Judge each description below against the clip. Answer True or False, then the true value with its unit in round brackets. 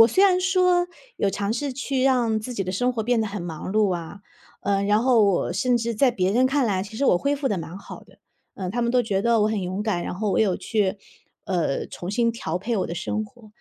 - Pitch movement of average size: True (4.1 semitones)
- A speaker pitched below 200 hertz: False (215 Hz)